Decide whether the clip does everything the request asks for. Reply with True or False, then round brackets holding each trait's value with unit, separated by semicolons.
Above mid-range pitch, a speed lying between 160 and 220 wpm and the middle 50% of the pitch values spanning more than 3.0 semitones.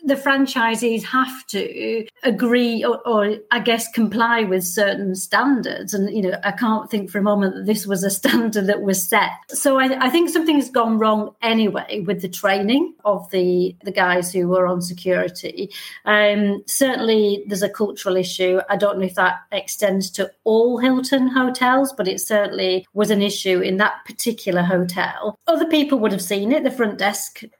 True (210 Hz; 185 wpm; 3.6 semitones)